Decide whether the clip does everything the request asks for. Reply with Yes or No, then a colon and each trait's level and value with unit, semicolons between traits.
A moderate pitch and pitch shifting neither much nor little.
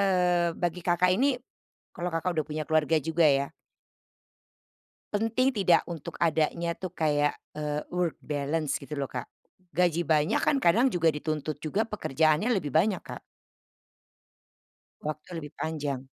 Yes: medium, 160 Hz; average, 3.1 semitones